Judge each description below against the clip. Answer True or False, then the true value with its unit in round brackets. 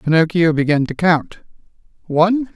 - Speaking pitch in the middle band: True (170 Hz)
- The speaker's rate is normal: False (115 wpm)